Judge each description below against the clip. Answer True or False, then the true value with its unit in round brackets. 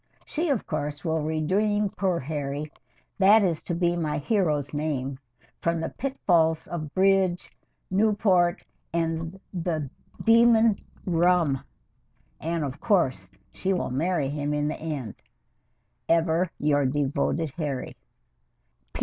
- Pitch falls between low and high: True (165 Hz)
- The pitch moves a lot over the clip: False (4.0 semitones)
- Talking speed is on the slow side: True (120 wpm)